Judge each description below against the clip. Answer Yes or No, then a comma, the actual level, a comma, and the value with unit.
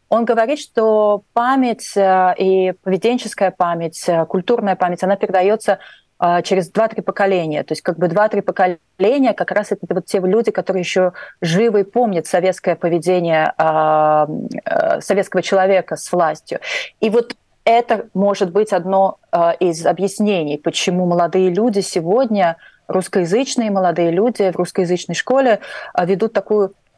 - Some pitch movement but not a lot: Yes, average, 3.2 semitones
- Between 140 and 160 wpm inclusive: No, average, 125 wpm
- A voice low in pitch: No, high, 190 Hz